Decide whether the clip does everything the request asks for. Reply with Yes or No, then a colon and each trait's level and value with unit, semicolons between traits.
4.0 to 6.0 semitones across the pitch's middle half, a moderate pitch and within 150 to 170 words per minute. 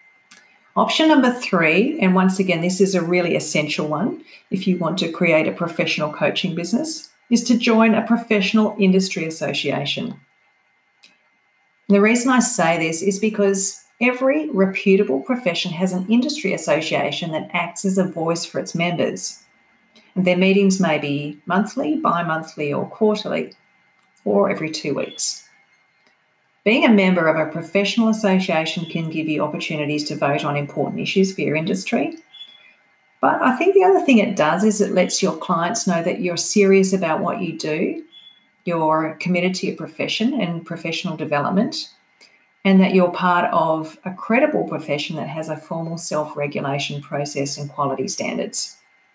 Yes: average, 4.7 semitones; medium, 180 Hz; average, 160 wpm